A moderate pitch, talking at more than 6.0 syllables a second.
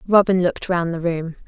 No: medium, 175 Hz; 5.5 syllables/s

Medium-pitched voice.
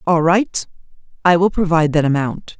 Yes: medium, 170 Hz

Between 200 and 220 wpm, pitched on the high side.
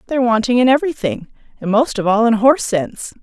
Yes: fast, 205 wpm; high, 235 Hz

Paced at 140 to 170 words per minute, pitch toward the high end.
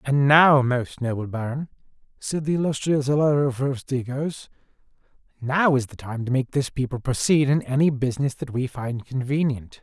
No: average, 160 wpm; low, 135 Hz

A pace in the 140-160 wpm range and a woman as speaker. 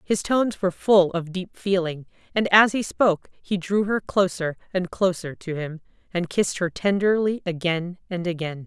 No: average, 180 wpm; female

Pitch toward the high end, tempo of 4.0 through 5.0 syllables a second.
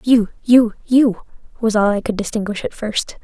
Yes: high, 220 Hz; 4.8 syllables/s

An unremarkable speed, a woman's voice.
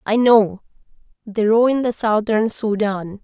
No: slow, 130 wpm; female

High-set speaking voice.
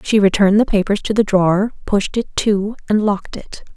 Yes: high, 205 Hz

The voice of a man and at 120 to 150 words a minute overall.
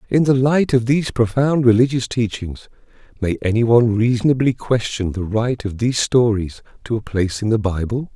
No: male; average, 175 wpm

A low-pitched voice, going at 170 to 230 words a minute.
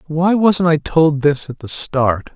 No: medium, 155 Hz; fast, 205 wpm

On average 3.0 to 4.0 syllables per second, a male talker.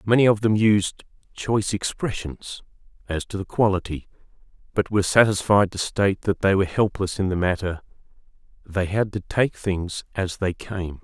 No: 5.0 syllables/s; male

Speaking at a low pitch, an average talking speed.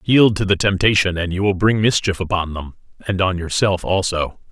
Yes: very low, 95 Hz; average, 185 wpm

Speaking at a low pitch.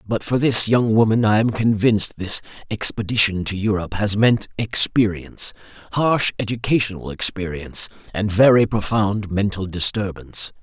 Yes: low, 105 Hz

